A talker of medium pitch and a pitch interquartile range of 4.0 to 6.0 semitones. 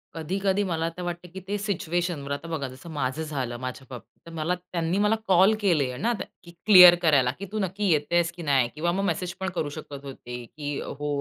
Yes: medium, 165 Hz; average, 4.3 semitones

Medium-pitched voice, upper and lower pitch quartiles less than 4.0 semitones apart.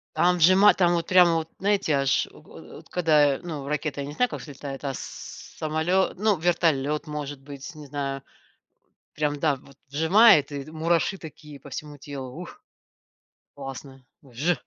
Yes: medium, 150 Hz; average, 3.5 semitones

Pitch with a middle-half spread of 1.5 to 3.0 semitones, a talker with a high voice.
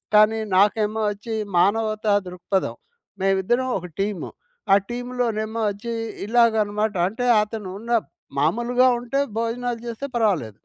Yes: average, 2.7 semitones; high, 220 Hz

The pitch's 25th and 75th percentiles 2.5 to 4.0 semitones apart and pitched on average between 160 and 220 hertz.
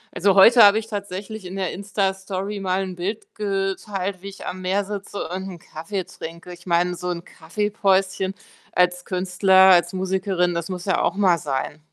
No: narrow, 1.8 semitones; high, 190 Hz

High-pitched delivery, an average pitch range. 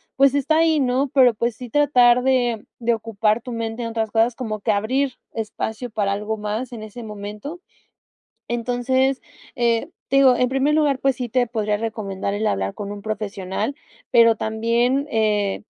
Yes: high, 230 Hz; average, 3.3 semitones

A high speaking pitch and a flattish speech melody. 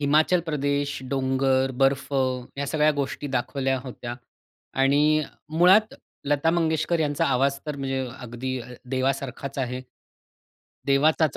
No: medium, 140 Hz; narrow, 2.2 semitones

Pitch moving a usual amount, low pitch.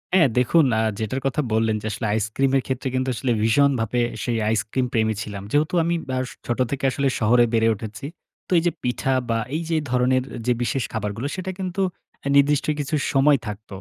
Yes: average, 4.0 semitones; low, 130 Hz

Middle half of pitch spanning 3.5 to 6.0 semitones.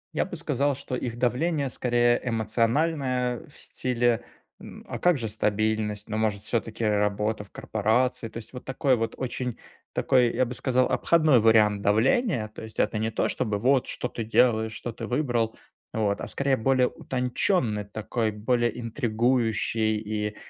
No: average, 2.7 semitones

